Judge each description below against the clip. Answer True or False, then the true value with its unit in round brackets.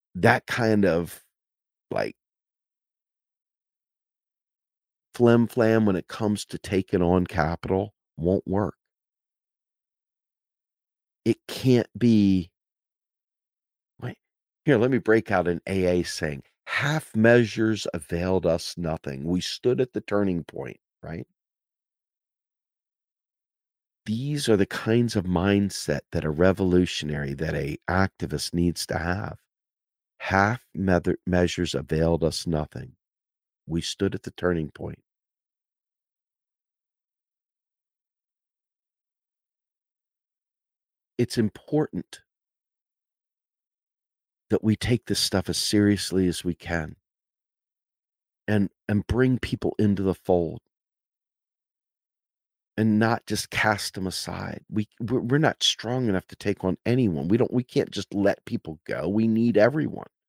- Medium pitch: False (95 Hz)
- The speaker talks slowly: True (110 wpm)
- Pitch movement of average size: True (4.3 semitones)